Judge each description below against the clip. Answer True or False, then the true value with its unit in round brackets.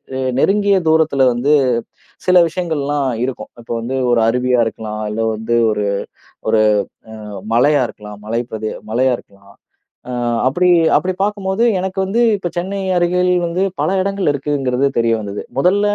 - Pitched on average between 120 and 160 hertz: True (140 Hz)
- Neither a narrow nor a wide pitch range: False (7.9 semitones)